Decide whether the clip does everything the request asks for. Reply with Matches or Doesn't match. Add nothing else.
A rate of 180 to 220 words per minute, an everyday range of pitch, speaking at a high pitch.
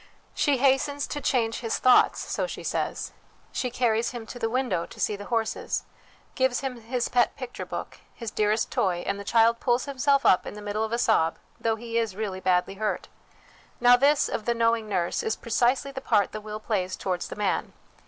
Matches